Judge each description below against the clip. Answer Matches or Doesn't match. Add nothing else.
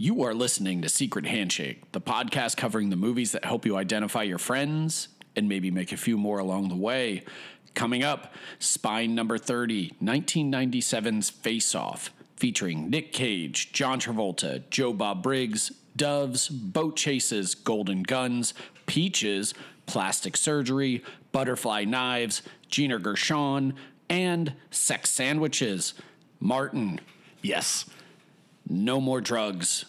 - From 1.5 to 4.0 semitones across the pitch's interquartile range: Doesn't match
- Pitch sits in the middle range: Doesn't match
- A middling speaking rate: Doesn't match